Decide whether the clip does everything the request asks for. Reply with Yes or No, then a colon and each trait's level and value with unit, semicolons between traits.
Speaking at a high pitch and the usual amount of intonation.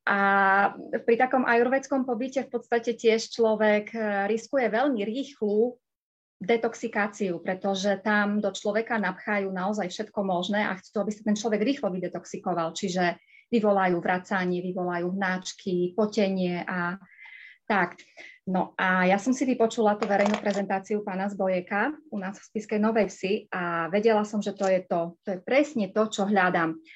Yes: high, 205 Hz; average, 3.1 semitones